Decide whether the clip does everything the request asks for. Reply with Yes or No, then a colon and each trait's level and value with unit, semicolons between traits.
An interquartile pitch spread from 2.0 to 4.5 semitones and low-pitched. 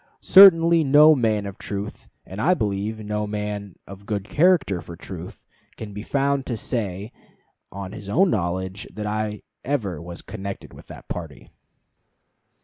No: average, 4.9 semitones; low, 105 Hz